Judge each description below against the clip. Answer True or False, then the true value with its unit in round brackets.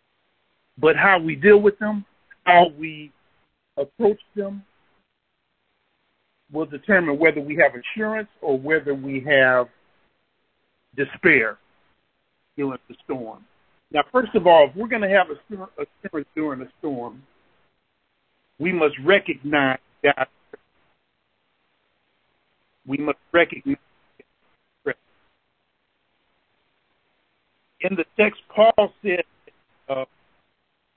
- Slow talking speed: True (100 wpm)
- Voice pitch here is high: False (165 Hz)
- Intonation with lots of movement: True (6.2 semitones)